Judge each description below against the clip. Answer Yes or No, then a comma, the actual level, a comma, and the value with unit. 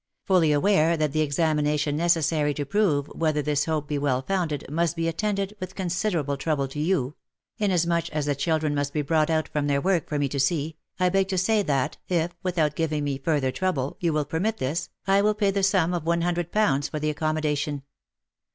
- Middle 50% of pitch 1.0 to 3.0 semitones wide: No, average, 3.4 semitones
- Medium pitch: Yes, medium, 155 Hz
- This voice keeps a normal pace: No, fast, 215 wpm